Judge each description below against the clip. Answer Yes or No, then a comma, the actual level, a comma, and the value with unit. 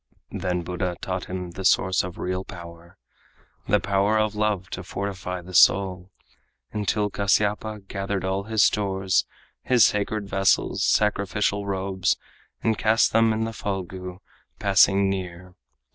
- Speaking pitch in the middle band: No, very low, 95 Hz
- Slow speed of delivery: Yes, slow, 130 wpm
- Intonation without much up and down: Yes, narrow, 2.1 semitones